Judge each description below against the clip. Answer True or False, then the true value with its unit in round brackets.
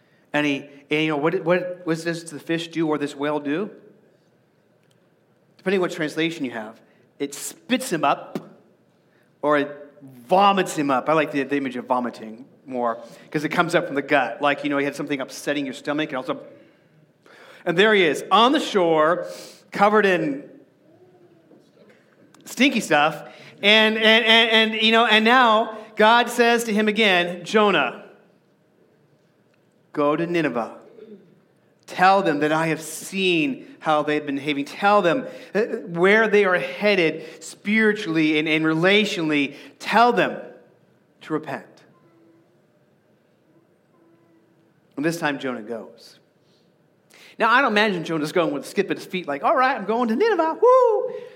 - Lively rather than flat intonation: True (6.4 semitones)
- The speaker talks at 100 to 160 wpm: True (155 wpm)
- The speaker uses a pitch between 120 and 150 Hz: False (170 Hz)